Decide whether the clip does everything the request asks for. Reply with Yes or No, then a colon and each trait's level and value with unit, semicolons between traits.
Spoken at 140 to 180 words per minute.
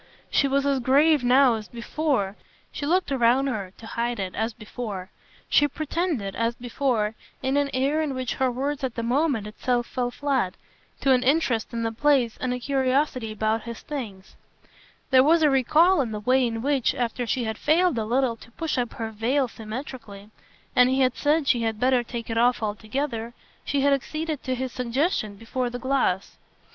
No: average, 195 wpm